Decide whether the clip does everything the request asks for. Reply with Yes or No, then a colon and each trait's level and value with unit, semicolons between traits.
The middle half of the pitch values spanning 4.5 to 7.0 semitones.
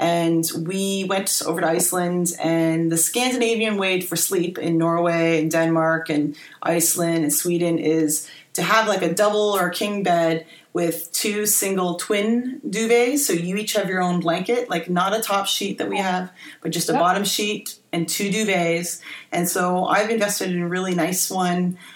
No: average, 3.2 semitones